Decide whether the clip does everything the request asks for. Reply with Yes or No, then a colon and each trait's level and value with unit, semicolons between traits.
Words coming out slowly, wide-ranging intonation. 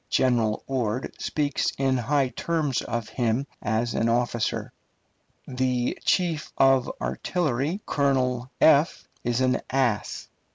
No: slow, 110 wpm; narrow, 2.5 semitones